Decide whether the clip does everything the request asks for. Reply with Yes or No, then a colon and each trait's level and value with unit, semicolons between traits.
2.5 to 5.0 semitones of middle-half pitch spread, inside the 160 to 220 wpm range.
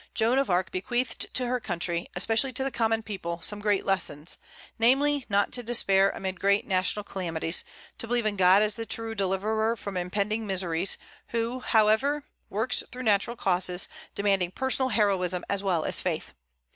Yes: average, 3.7 semitones; average, 170 wpm